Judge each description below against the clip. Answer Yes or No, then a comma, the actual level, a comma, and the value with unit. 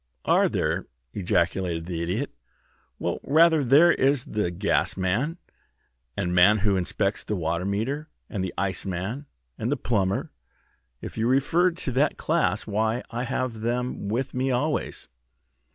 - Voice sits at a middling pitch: No, low, 110 Hz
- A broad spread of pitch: Yes, wide, 6.1 semitones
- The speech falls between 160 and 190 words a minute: No, average, 140 wpm